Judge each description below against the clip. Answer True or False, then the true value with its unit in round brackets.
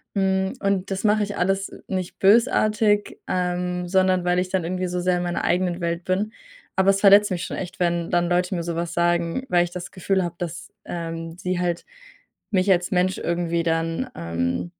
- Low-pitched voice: False (180 Hz)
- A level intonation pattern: True (1.8 semitones)